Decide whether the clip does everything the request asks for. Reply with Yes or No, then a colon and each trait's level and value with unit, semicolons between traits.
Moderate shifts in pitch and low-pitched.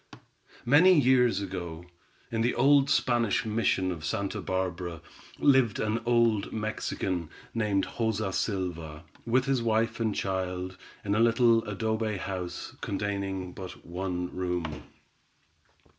Yes: average, 4.0 semitones; low, 105 Hz